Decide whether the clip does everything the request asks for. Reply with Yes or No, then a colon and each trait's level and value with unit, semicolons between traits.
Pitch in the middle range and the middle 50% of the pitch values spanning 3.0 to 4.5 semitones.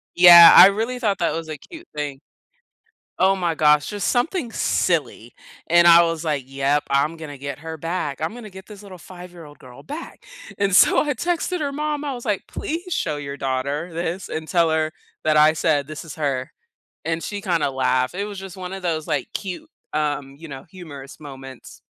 No: medium, 165 Hz; average, 5.0 semitones